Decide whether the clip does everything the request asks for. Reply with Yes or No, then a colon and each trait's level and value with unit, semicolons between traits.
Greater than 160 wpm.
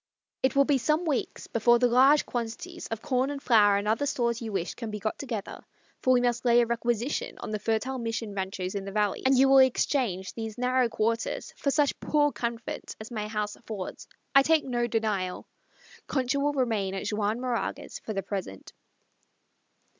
Yes: average, 190 wpm